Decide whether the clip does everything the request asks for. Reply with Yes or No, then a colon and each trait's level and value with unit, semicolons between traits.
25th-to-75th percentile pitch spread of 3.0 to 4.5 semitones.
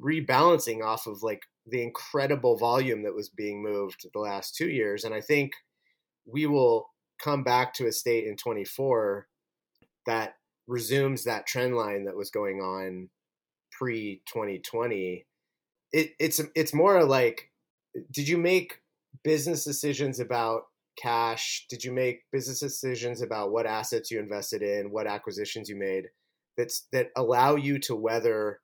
No: average, 5.3 semitones